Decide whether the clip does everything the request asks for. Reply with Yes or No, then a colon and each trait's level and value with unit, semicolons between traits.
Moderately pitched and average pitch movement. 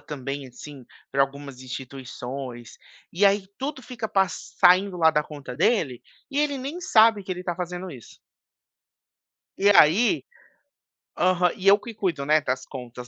No: medium, 170 Hz; wide, 6.8 semitones